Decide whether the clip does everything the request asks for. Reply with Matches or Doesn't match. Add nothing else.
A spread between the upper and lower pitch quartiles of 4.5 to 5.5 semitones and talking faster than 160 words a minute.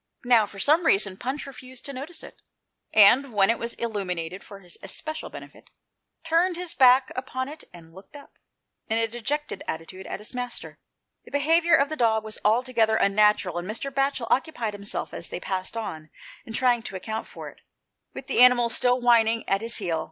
Matches